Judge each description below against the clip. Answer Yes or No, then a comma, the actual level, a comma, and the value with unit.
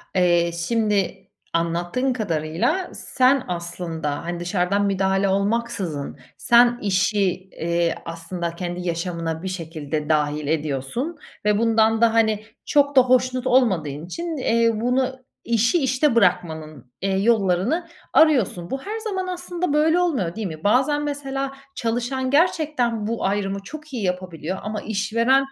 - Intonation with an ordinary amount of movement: No, wide, 6.9 semitones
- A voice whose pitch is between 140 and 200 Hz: No, high, 210 Hz